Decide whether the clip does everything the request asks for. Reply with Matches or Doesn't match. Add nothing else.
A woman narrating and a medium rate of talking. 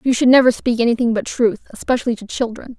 Doesn't match